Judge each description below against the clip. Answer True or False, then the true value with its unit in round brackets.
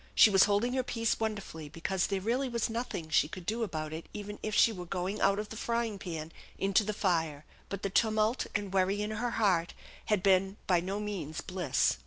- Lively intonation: False (3.3 semitones)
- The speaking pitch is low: False (200 Hz)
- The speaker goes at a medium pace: False (215 wpm)